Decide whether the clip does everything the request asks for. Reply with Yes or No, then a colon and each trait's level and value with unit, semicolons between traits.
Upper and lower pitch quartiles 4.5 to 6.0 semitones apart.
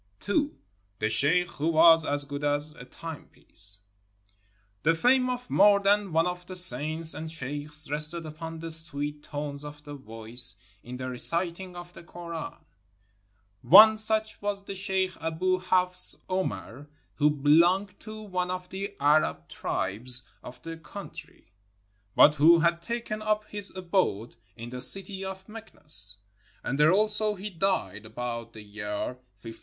Yes: average, 5.0 semitones